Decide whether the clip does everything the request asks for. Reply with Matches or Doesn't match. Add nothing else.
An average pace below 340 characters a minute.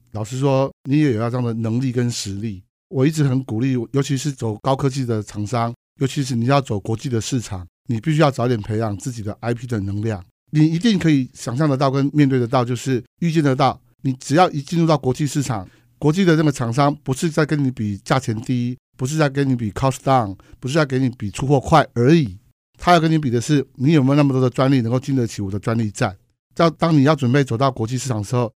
Doesn't match